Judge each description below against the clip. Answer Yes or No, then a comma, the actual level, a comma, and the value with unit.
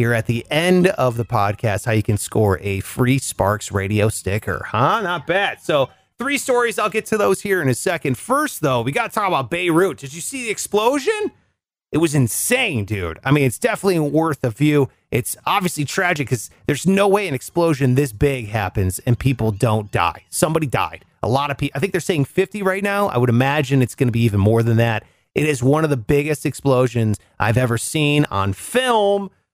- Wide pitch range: Yes, wide, 8.2 semitones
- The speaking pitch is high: No, low, 135 Hz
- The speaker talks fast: Yes, fast, 215 wpm